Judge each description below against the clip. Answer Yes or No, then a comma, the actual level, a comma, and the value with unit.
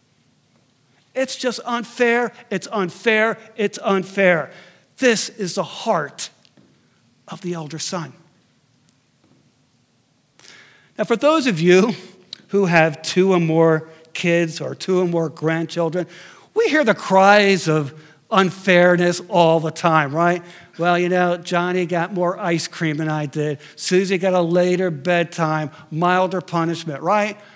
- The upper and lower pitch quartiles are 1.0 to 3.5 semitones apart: Yes, average, 3.0 semitones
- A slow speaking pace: Yes, slow, 130 wpm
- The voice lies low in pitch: No, medium, 180 Hz